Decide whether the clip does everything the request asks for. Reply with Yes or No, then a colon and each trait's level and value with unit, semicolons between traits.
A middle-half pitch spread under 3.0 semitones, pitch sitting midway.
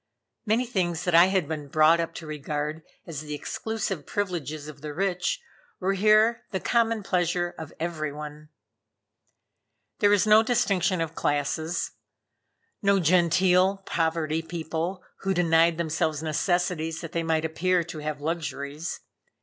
No: average, 3.3 semitones; medium, 170 Hz